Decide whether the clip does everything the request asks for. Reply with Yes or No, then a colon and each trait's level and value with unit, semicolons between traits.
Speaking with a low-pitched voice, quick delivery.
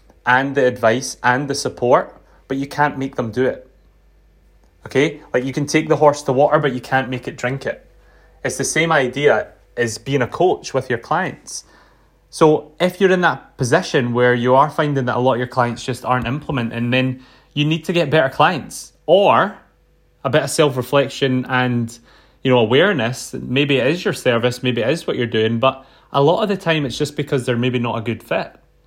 Yes: low, 130 Hz; fast, 210 wpm